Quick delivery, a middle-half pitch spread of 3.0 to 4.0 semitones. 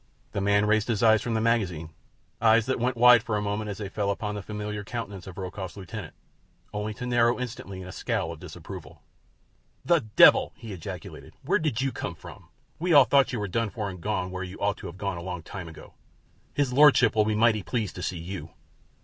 Yes: fast, 220 wpm; average, 3.5 semitones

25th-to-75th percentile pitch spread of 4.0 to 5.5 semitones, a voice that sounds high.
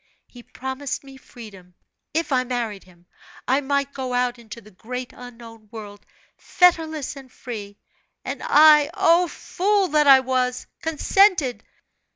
Yes: average, 4.3 semitones; very high, 255 Hz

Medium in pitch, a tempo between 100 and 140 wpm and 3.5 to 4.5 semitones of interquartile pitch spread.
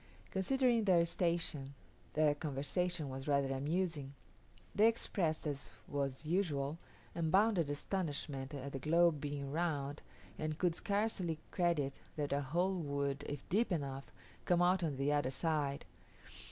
Yes: medium, 155 Hz; slow, 135 wpm; average, 4.0 semitones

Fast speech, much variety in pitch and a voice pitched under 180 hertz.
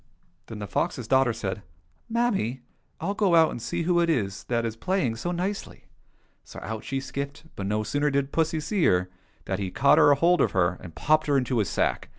Yes: fast, 220 wpm; wide, 7.7 semitones; low, 135 Hz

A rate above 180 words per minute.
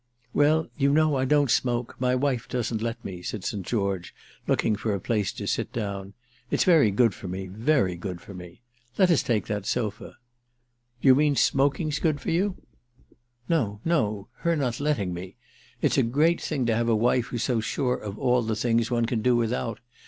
Yes: average, 190 wpm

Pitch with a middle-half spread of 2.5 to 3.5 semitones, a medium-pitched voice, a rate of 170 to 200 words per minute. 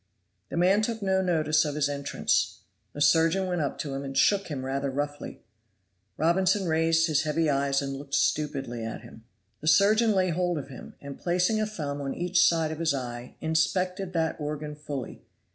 No: average, 4.2 semitones; medium, 155 Hz; average, 190 wpm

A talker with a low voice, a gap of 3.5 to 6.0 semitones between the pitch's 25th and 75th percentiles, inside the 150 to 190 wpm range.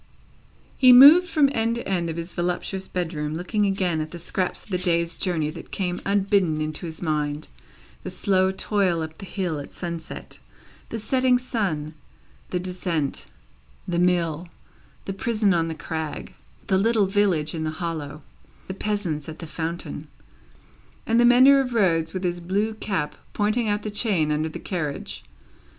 No: medium, 180 Hz; average, 4.3 semitones; average, 170 wpm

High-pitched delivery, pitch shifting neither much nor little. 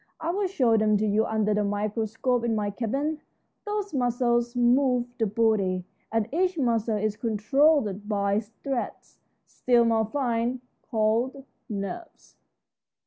Yes: high, 230 Hz; average, 3.5 semitones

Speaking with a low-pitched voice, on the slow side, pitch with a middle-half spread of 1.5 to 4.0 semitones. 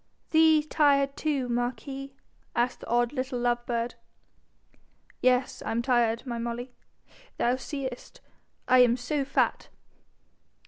No: very high, 250 Hz; slow, 125 wpm; narrow, 2.4 semitones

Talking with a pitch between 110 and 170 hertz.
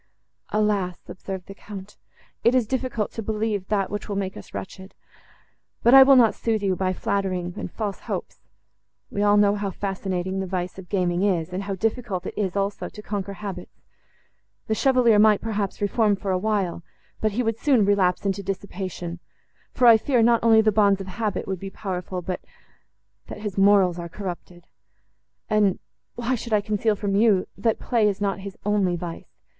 No: high, 200 Hz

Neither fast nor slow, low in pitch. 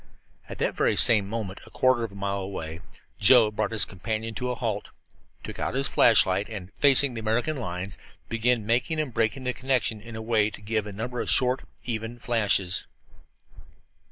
Yes: average, 185 wpm; low, 115 Hz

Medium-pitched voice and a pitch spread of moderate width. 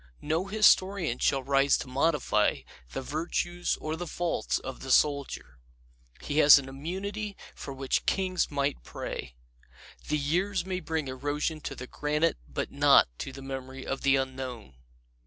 Yes: medium, 145 Hz; average, 4.5 semitones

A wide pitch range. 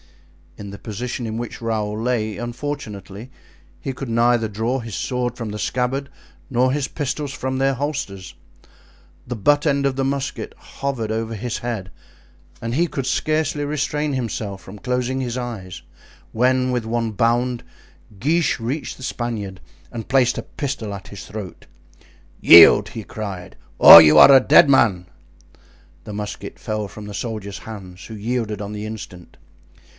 No: average, 3.9 semitones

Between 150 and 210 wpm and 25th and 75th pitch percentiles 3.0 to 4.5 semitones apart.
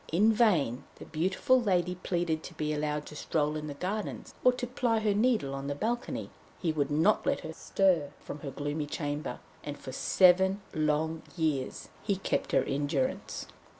No: average, 185 wpm; average, 5.2 semitones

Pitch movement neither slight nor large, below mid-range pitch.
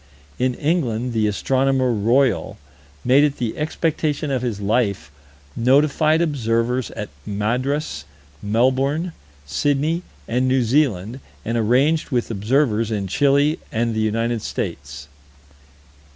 Yes: average, 4.4 semitones; low, 125 Hz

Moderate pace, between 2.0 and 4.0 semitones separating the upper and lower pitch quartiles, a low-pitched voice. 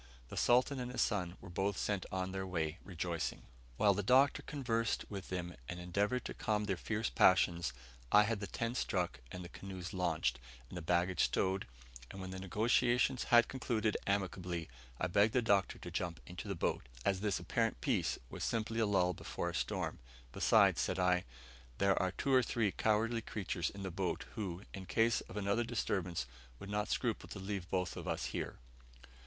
Yes: average, 190 wpm; average, 3.5 semitones; very low, 95 Hz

